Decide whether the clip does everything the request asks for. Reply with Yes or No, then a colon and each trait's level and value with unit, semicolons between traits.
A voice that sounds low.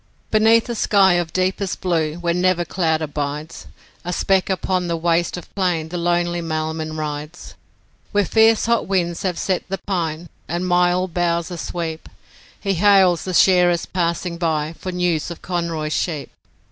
No: medium, 175 Hz